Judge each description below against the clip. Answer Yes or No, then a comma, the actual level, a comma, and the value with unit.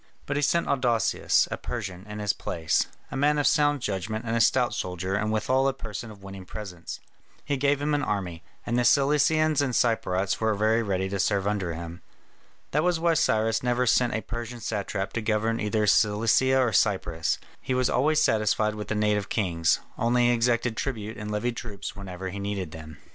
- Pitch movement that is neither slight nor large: Yes, average, 4.0 semitones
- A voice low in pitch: Yes, low, 110 Hz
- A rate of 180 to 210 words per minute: Yes, average, 195 wpm